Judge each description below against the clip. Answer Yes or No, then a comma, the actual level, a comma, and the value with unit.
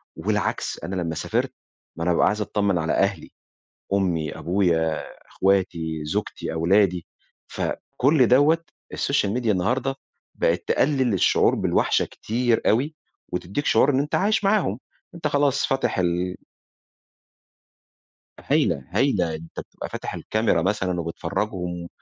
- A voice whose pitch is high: No, low, 100 Hz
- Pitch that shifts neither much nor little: No, wide, 7.0 semitones